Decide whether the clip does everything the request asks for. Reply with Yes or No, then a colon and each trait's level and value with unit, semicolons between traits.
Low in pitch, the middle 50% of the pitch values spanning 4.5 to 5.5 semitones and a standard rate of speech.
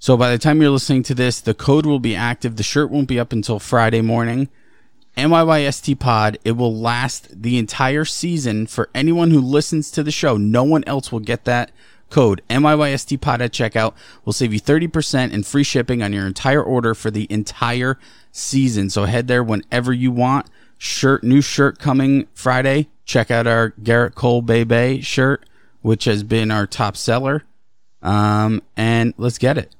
No: low, 125 Hz; average, 3.5 semitones; average, 185 wpm